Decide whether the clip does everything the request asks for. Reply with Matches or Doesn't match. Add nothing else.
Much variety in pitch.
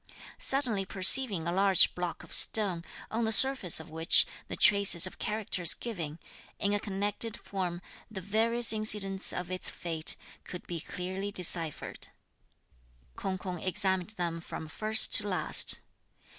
Doesn't match